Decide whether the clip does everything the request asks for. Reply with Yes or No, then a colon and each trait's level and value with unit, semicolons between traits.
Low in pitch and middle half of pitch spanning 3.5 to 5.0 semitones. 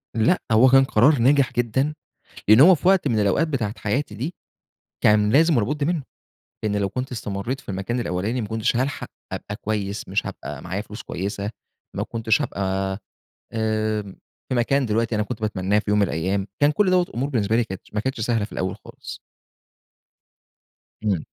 Yes: low, 110 Hz; average, 4.2 semitones